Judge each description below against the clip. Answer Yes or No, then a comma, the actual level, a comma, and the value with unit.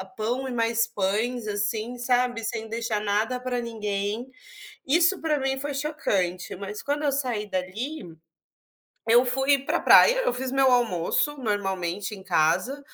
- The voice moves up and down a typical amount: Yes, average, 4.5 semitones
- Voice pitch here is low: No, high, 235 Hz